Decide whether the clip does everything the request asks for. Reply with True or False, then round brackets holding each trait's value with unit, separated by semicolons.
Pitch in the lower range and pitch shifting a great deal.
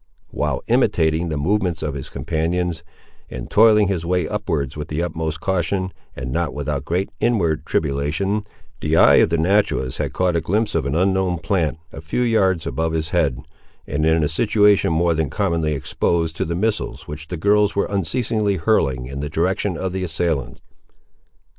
False (85 Hz; 3.7 semitones)